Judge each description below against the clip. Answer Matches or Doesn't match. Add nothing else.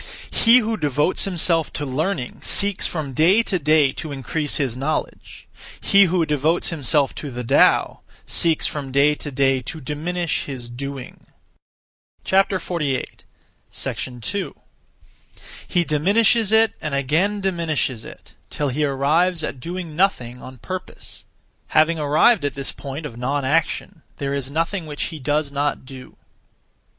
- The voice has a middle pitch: Matches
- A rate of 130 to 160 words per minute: Matches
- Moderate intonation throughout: Matches